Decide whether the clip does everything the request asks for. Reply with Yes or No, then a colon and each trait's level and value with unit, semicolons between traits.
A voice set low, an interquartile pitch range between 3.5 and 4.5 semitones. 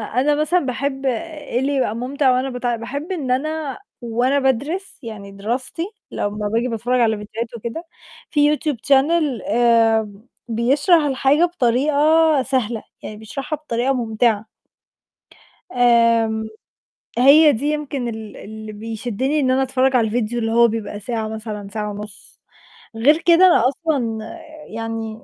No: high, 245 Hz; average, 4.0 semitones